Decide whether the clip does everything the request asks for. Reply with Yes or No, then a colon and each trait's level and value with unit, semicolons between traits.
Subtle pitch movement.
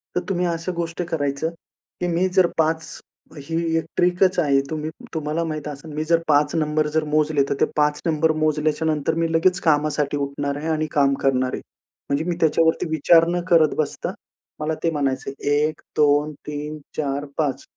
Yes: narrow, 2.0 semitones